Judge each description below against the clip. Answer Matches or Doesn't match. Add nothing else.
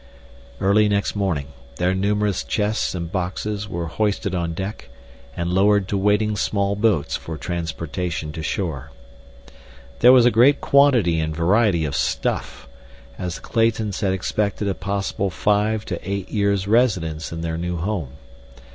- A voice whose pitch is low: Matches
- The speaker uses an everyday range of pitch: Matches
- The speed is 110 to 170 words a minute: Matches